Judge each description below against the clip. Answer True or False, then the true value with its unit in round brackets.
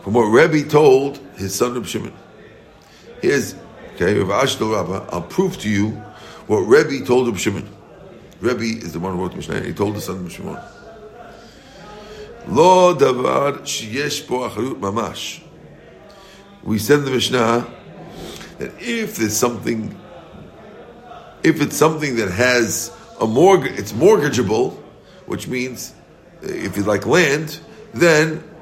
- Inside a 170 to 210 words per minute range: False (135 wpm)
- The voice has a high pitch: False (135 Hz)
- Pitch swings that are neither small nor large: False (8.0 semitones)